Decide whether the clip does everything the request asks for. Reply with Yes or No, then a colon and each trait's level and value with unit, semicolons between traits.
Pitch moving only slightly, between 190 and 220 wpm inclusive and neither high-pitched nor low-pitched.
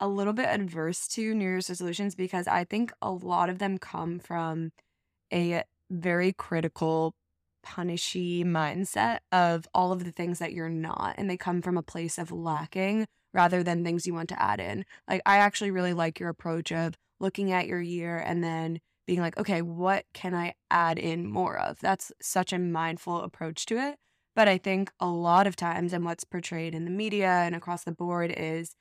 Yes: narrow, 1.9 semitones; average, 200 wpm; medium, 175 Hz